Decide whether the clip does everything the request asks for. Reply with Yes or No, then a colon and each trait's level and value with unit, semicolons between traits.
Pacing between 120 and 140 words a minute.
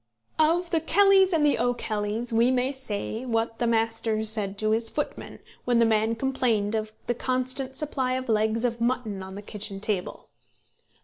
No: average, 175 wpm